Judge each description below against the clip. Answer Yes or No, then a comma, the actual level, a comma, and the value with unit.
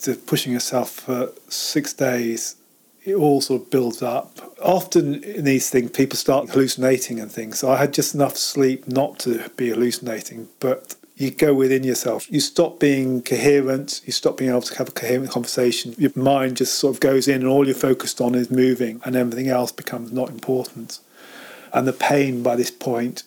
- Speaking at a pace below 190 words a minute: No, average, 195 wpm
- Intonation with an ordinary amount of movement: No, narrow, 2.0 semitones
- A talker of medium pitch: No, low, 130 Hz